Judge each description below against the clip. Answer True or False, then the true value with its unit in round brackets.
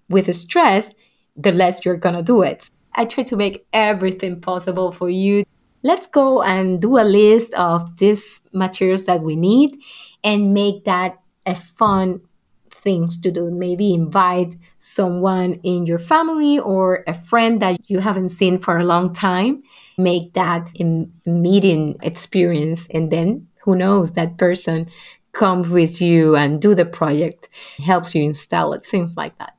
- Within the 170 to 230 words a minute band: False (160 wpm)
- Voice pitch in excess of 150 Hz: True (185 Hz)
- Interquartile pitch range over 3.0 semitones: False (2.7 semitones)